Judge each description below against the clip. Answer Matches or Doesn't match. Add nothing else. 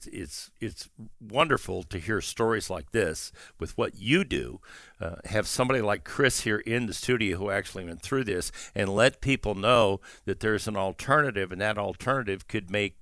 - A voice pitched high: Doesn't match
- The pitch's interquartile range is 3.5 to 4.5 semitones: Matches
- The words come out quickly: Doesn't match